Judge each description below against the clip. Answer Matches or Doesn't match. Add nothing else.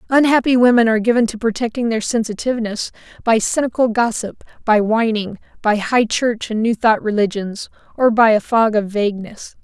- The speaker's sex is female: Matches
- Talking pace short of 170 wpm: Matches